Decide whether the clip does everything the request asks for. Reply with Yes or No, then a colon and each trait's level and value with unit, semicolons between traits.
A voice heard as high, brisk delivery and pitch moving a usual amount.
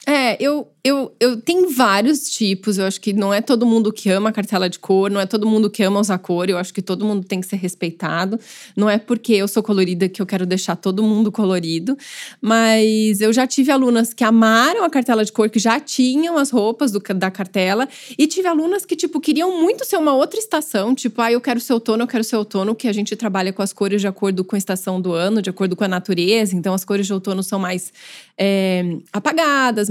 Yes: high, 215 Hz; fast, 235 wpm; average, 4.5 semitones